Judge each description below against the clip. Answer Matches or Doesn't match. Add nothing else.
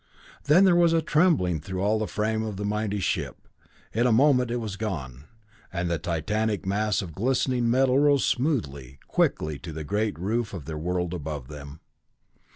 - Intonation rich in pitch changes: Matches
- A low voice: Matches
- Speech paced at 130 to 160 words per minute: Doesn't match